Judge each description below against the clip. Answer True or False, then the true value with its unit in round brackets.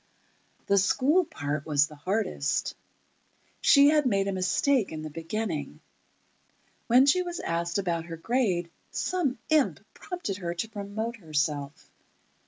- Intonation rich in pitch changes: True (7.7 semitones)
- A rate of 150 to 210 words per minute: False (135 wpm)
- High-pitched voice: True (195 Hz)